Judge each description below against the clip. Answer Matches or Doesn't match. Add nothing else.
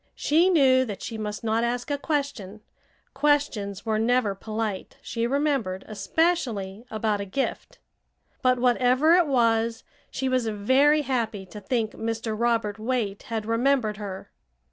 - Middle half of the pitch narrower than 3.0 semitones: Doesn't match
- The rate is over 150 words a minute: Doesn't match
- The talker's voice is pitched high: Matches